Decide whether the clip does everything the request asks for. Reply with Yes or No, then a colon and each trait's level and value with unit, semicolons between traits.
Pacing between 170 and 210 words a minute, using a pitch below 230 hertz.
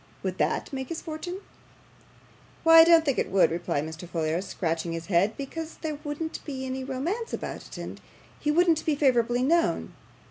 No: average, 180 wpm; very high, 270 Hz